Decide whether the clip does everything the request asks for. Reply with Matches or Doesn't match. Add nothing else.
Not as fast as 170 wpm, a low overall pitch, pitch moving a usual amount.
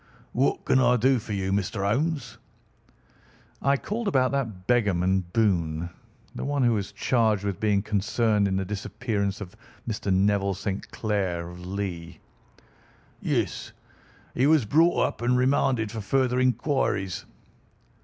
Matches